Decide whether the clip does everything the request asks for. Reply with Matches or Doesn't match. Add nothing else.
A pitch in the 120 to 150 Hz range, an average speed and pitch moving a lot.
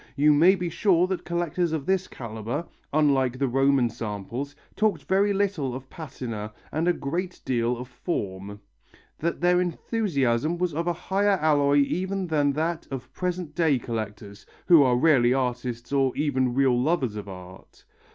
Matches